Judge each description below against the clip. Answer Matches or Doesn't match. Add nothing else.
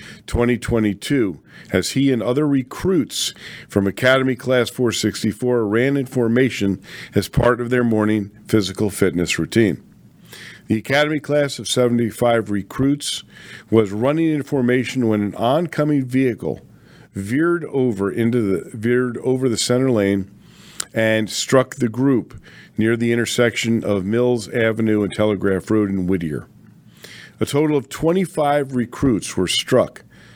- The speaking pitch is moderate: Doesn't match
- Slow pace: Matches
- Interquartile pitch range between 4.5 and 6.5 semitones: Doesn't match